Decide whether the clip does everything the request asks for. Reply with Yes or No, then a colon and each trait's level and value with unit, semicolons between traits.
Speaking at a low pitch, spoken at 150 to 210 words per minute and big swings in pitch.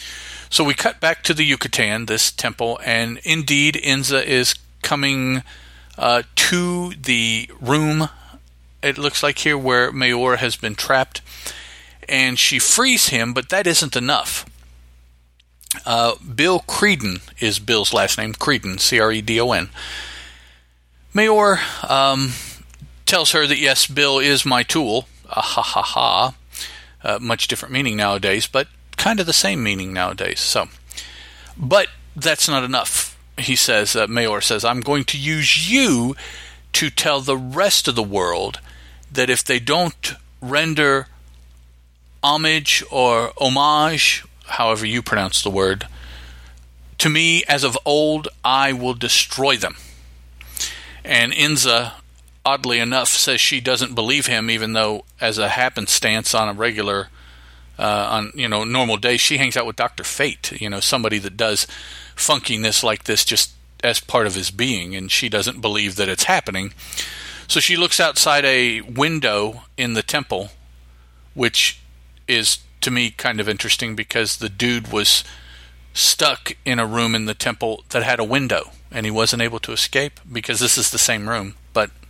Yes: low, 115 Hz; average, 155 wpm; wide, 7.1 semitones